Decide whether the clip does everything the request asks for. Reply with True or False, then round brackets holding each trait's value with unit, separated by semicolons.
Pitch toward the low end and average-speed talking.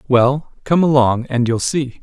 True (130 Hz; 180 wpm)